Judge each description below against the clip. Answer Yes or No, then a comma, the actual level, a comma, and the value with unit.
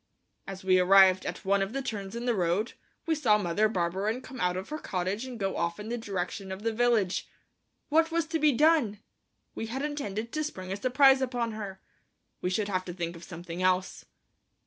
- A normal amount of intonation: Yes, average, 5.0 semitones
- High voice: Yes, high, 205 Hz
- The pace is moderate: No, fast, 210 wpm